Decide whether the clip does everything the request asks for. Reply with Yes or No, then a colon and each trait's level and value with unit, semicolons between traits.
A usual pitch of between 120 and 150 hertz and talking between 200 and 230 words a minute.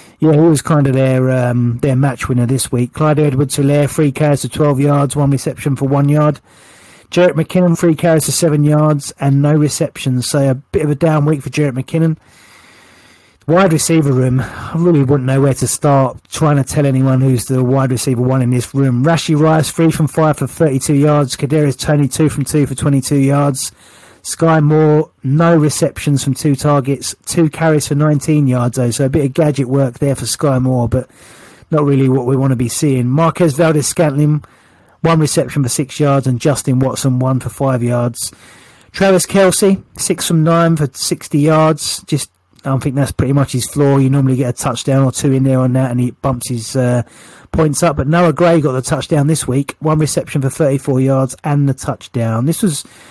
Yes: medium, 140 Hz; fast, 205 wpm